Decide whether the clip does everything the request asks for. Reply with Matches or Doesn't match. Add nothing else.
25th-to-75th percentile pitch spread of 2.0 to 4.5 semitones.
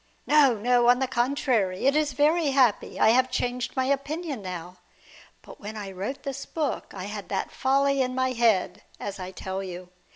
Doesn't match